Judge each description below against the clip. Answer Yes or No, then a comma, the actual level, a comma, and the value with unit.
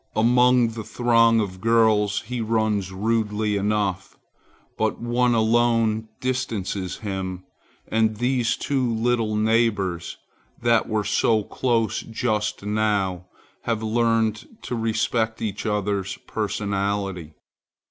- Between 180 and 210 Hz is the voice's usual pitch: No, low, 110 Hz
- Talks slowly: Yes, slow, 105 wpm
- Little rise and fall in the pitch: Yes, narrow, 2.2 semitones